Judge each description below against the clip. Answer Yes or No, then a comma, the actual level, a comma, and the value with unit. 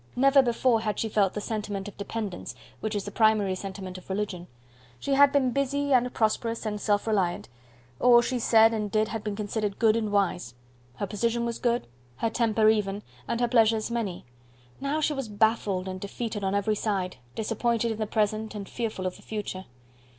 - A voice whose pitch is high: Yes, high, 215 Hz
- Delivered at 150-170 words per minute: No, average, 195 wpm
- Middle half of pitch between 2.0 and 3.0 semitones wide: Yes, narrow, 2.5 semitones